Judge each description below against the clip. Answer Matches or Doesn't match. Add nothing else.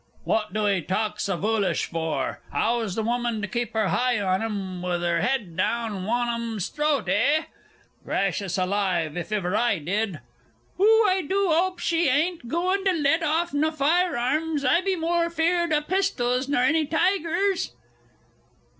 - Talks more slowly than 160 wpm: Doesn't match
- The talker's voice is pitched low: Doesn't match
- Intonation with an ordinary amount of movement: Doesn't match